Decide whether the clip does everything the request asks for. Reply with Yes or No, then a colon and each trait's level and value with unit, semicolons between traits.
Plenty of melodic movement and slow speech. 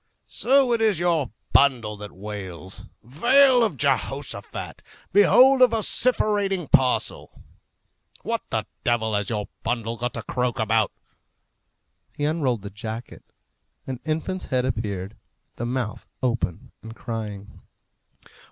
Yes: wide, 8.1 semitones; slow, 120 wpm